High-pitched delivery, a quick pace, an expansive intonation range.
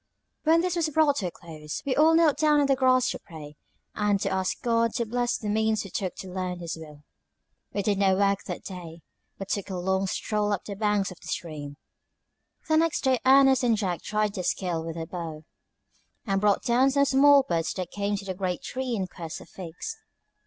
Yes: high, 200 Hz; fast, 220 wpm; wide, 6.3 semitones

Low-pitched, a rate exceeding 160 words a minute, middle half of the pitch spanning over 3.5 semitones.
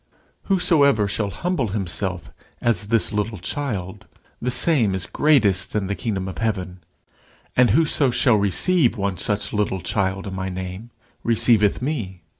No: low, 105 Hz; average, 145 wpm; average, 4.3 semitones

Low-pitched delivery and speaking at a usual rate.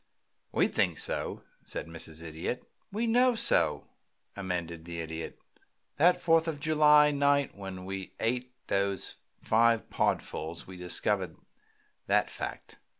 No: low, 100 Hz; slow, 125 wpm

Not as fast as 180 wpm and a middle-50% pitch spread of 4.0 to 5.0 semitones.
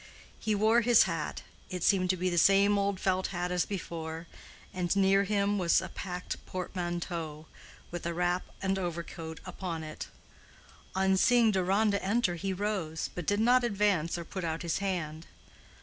No: average, 160 wpm; average, 2.7 semitones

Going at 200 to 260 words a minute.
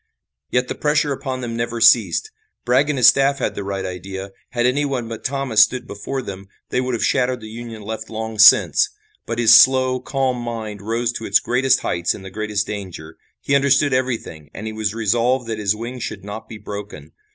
Yes: fast, 205 wpm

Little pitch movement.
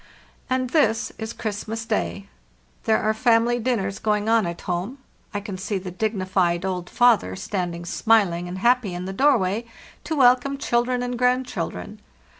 No: average, 4.7 semitones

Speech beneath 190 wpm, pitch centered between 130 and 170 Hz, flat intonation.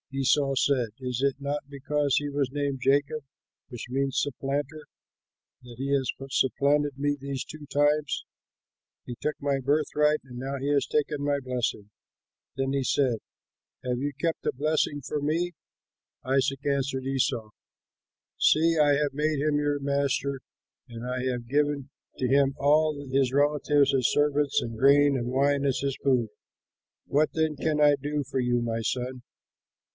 Yes: average, 160 wpm; medium, 140 Hz; narrow, 1.8 semitones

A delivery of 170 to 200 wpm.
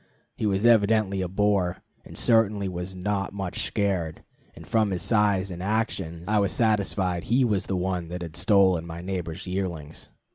Yes: average, 175 wpm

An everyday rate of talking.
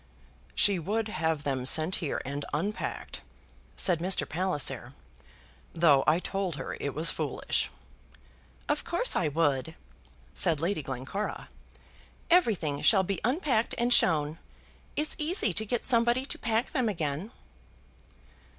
No: slow, 130 wpm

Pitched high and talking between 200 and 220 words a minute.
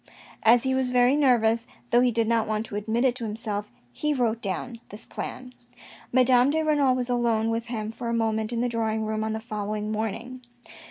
Yes: high, 230 Hz; fast, 205 wpm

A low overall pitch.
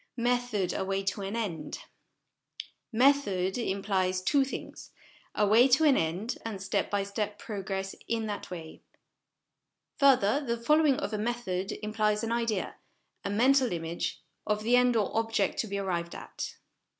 No: high, 210 Hz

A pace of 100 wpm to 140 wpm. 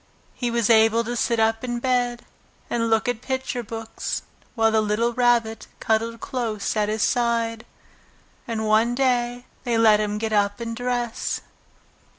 No: average, 160 wpm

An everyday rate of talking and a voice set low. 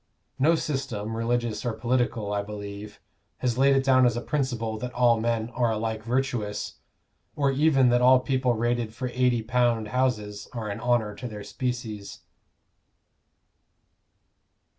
Yes: average, 145 wpm; low, 120 Hz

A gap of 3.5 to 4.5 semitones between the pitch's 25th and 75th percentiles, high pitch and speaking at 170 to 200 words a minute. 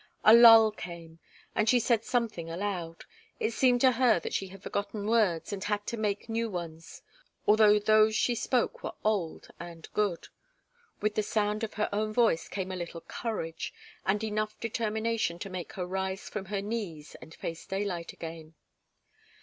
Yes: average, 3.9 semitones; high, 205 Hz; average, 175 wpm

